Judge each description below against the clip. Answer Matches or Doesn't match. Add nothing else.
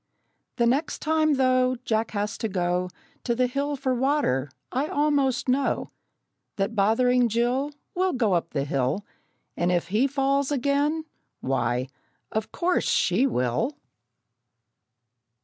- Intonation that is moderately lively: Doesn't match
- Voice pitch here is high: Matches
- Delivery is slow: Matches